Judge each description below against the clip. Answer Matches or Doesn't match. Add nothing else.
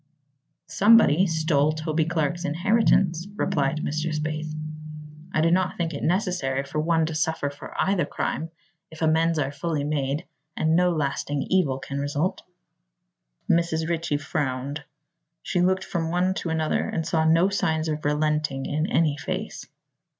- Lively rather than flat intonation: Doesn't match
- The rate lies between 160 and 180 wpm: Doesn't match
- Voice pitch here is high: Doesn't match